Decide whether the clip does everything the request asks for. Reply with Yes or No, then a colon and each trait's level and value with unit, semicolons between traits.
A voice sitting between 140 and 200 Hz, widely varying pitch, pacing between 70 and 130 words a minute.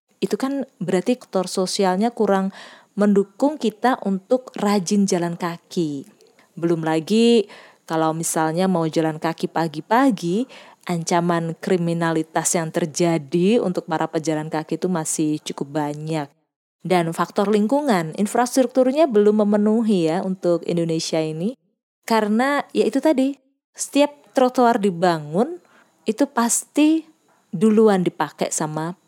Yes: high, 190 Hz; wide, 6.0 semitones; average, 110 wpm